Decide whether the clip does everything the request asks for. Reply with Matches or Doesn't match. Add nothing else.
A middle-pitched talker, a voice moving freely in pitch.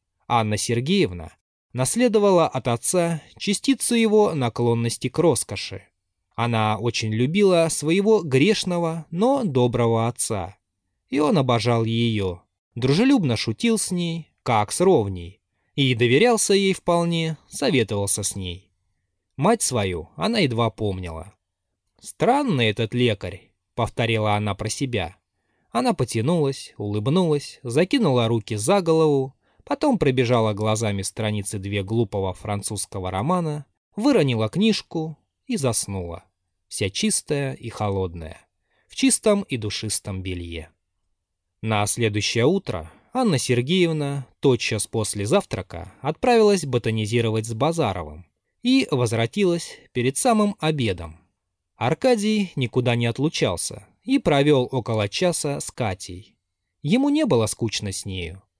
Doesn't match